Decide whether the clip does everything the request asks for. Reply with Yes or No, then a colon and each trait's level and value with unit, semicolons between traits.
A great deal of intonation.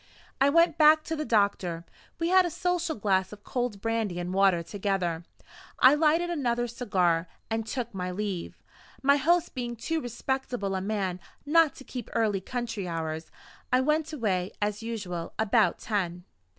Yes: wide, 6.9 semitones